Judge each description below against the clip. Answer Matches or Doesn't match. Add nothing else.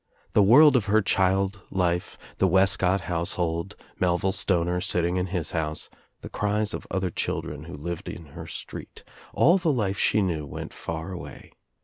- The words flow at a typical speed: Matches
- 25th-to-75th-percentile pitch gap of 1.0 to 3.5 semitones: Matches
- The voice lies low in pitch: Matches